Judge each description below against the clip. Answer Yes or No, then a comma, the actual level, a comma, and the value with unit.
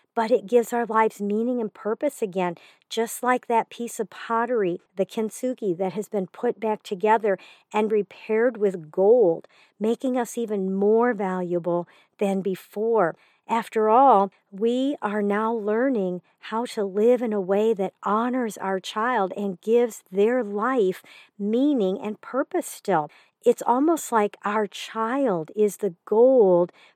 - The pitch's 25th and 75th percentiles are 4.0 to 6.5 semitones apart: No, average, 3.0 semitones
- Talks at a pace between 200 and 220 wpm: No, average, 145 wpm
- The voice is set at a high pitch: Yes, high, 220 Hz